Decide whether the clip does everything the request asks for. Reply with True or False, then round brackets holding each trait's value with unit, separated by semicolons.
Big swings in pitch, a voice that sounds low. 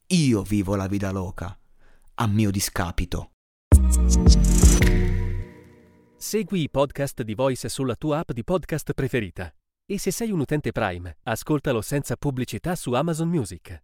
True (8.1 semitones; 110 Hz)